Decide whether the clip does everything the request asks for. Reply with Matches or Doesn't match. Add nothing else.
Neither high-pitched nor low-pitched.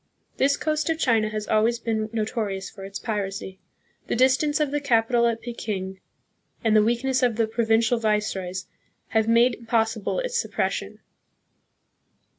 Doesn't match